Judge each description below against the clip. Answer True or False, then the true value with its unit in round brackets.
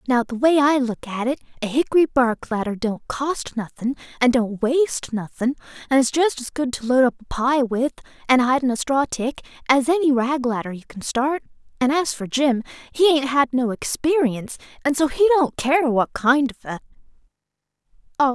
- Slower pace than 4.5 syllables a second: False (5.1 syllables/s)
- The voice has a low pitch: False (260 Hz)